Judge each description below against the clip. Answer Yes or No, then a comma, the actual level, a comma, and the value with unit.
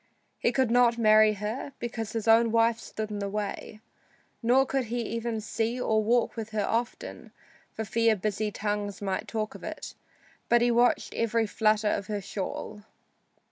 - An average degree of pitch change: No, narrow, 1.8 semitones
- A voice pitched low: No, high, 220 Hz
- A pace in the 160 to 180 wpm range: Yes, average, 175 wpm